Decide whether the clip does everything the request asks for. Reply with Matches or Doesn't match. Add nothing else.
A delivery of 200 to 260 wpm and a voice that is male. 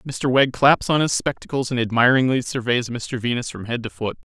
Matches